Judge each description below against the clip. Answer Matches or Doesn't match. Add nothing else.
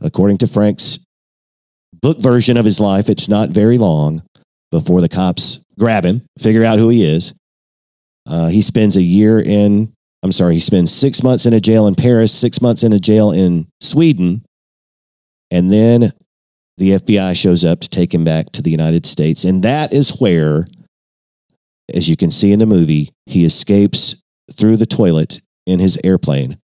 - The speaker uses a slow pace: Doesn't match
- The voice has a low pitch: Matches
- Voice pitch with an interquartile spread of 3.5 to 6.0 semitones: Matches